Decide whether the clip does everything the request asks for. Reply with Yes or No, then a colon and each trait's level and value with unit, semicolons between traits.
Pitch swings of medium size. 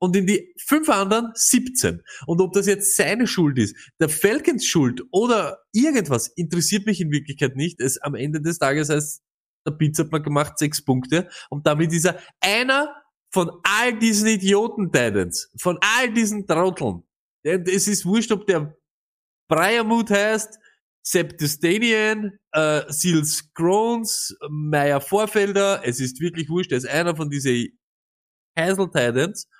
No: wide, 6.0 semitones